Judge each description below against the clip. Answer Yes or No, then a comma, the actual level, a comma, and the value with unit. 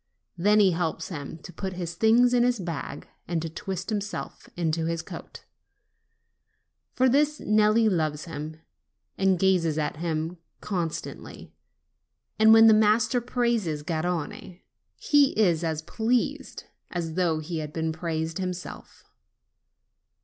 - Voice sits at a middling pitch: Yes, medium, 180 Hz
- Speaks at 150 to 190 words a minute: No, slow, 135 wpm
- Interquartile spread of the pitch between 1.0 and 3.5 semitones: No, average, 5.0 semitones